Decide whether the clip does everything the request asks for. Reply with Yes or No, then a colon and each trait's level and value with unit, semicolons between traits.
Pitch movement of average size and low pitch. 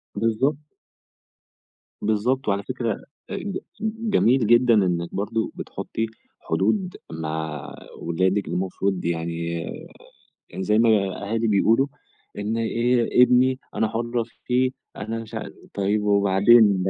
Yes: average, 4.0 semitones; low, 110 Hz